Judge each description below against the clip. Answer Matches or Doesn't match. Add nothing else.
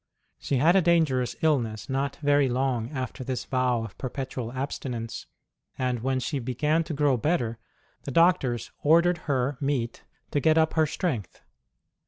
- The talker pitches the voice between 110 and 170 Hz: Matches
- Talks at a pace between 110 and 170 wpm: Matches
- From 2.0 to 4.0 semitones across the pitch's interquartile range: Matches